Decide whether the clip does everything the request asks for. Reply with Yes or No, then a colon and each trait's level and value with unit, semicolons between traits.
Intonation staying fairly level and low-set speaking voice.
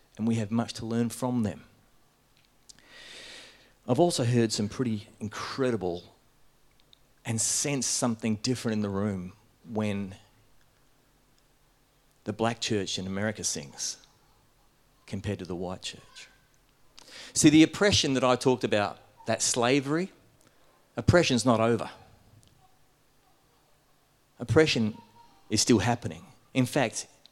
No: average, 3.6 semitones; low, 120 Hz